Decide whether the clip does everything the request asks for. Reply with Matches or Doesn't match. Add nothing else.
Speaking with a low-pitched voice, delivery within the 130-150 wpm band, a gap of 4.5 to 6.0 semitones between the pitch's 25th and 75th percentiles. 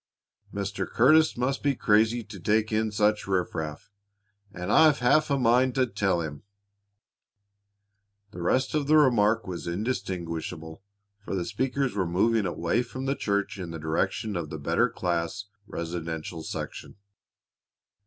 Matches